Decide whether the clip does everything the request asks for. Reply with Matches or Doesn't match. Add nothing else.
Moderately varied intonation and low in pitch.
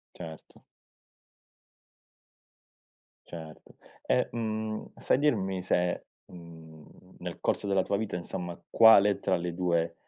Matches